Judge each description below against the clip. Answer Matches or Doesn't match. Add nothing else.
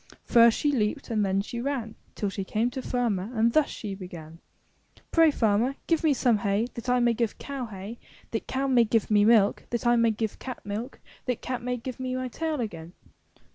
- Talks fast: Matches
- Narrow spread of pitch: Doesn't match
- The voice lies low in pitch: Doesn't match